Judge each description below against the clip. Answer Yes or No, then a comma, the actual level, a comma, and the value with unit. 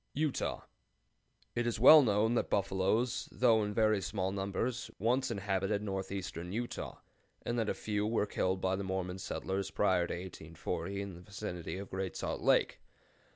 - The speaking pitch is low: Yes, low, 100 Hz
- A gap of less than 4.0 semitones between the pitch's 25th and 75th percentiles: Yes, average, 2.9 semitones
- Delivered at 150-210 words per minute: Yes, average, 160 wpm